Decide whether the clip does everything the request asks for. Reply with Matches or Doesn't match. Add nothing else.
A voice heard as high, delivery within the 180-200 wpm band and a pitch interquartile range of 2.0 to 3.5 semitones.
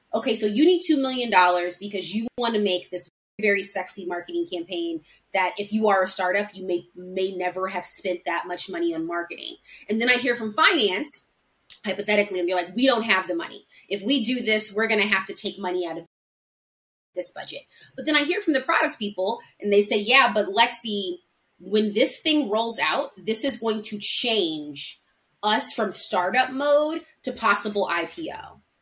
Doesn't match